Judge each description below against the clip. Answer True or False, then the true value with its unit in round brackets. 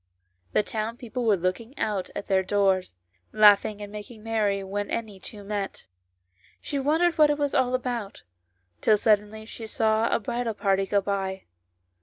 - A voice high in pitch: True (210 Hz)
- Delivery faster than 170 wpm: False (160 wpm)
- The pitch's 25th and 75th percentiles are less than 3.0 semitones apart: True (2.6 semitones)